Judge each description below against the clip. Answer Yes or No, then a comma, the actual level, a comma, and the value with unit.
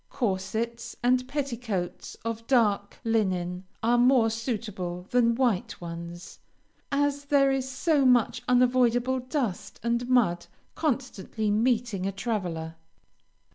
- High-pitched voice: Yes, high, 235 Hz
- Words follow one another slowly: Yes, slow, 110 wpm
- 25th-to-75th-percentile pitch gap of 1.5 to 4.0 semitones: No, average, 4.5 semitones